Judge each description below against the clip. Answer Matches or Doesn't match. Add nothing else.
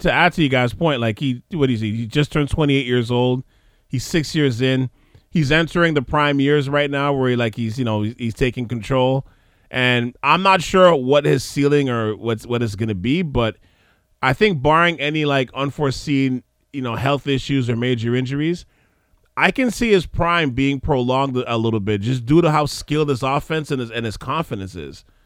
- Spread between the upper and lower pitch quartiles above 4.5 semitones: Doesn't match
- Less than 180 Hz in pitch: Matches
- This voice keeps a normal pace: Doesn't match